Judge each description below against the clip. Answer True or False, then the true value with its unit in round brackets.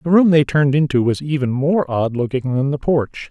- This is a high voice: False (140 Hz)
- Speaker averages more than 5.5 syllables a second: False (5.4 syllables/s)